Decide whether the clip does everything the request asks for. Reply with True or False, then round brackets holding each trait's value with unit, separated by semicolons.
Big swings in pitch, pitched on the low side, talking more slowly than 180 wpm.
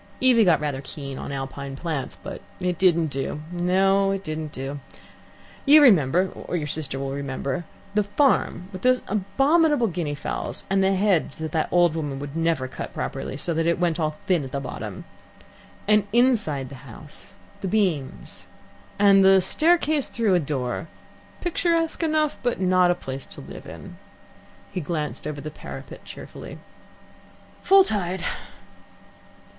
False (5.8 semitones; 175 Hz; 160 wpm)